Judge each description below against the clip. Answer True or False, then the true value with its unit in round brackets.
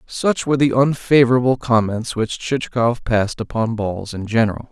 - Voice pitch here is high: False (120 Hz)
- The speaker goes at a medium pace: True (155 wpm)